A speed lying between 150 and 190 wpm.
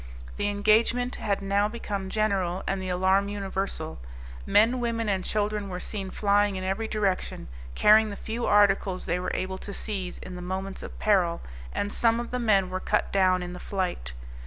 Yes: average, 185 wpm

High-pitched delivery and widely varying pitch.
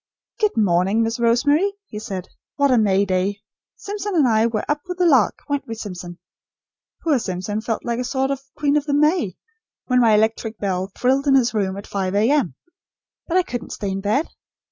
Yes: high, 230 Hz; wide, 5.9 semitones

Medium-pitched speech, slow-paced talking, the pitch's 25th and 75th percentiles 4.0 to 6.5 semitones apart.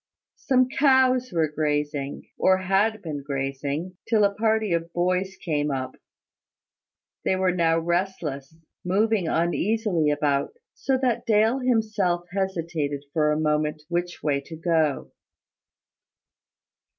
Yes: medium, 175 Hz; slow, 120 wpm; wide, 5.5 semitones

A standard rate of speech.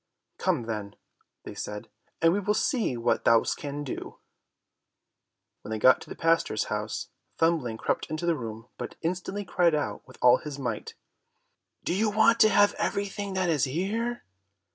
Yes: average, 165 wpm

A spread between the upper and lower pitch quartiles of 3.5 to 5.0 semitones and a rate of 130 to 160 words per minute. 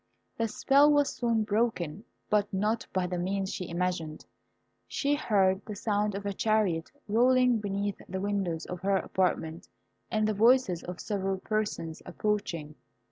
No: average, 3.1 semitones; average, 150 wpm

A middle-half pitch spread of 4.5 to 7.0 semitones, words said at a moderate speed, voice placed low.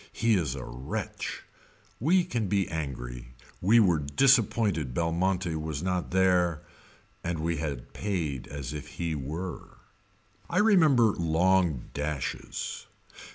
No: average, 5.0 semitones; slow, 120 wpm; very low, 85 Hz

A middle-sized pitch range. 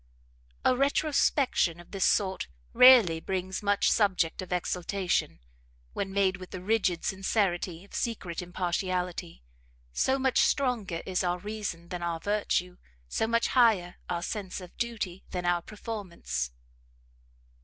Yes: average, 3.2 semitones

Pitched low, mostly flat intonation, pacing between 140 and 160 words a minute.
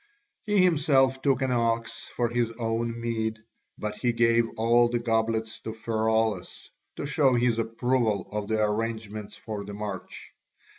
Yes: low, 115 Hz; narrow, 1.5 semitones; average, 150 wpm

